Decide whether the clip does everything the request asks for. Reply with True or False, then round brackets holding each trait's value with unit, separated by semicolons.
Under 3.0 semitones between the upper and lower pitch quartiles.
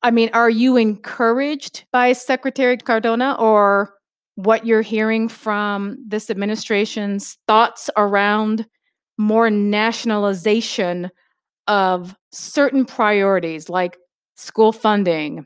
True (2.4 semitones)